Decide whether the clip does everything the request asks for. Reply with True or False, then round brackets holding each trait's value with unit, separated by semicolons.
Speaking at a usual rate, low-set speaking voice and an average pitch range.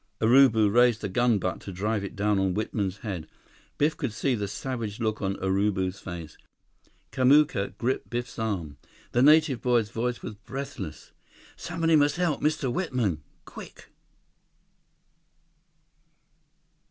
False (130 wpm; 110 Hz; 4.9 semitones)